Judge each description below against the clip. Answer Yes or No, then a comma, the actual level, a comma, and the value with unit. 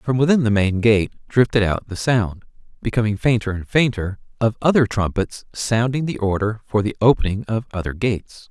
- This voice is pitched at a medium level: No, low, 110 Hz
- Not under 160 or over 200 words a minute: Yes, average, 175 wpm